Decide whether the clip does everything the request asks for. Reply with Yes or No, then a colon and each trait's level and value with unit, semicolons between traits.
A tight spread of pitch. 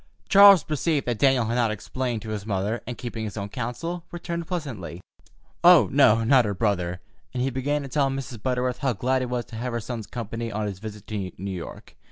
No: average, 3.9 semitones